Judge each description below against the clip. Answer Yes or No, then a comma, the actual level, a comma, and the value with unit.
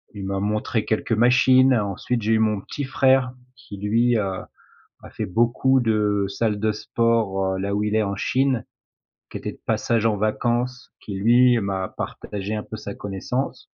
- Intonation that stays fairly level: No, average, 3.1 semitones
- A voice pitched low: Yes, low, 110 Hz